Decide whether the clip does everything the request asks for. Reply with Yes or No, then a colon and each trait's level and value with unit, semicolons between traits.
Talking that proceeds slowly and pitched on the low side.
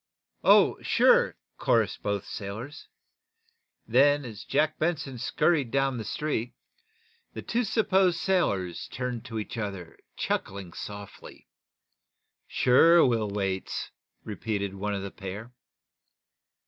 Yes: slow, 110 wpm; low, 115 Hz